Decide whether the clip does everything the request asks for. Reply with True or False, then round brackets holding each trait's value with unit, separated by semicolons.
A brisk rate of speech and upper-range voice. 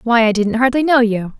True (260 wpm; 235 Hz)